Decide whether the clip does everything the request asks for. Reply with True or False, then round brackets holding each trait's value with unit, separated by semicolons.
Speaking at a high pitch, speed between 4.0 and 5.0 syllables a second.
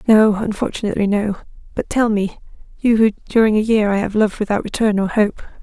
False (210 Hz; 6.2 syllables/s)